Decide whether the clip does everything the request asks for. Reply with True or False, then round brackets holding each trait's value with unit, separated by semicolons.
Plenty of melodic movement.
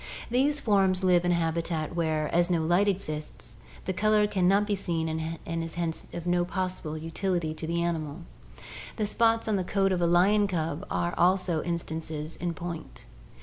False (2.9 semitones)